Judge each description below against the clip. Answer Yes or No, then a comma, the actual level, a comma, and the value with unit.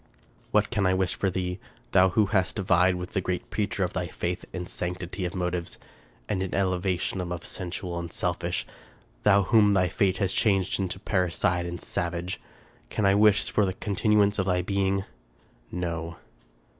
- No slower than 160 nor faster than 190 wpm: Yes, average, 175 wpm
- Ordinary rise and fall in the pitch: No, narrow, 1.7 semitones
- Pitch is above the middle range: No, very low, 95 Hz